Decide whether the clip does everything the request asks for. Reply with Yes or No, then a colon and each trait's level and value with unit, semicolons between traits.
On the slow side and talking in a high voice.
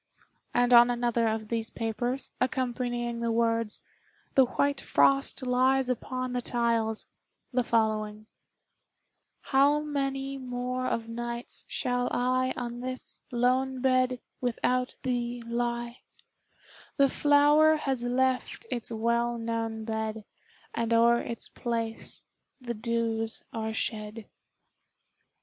Yes: slow, 115 wpm; high, 240 Hz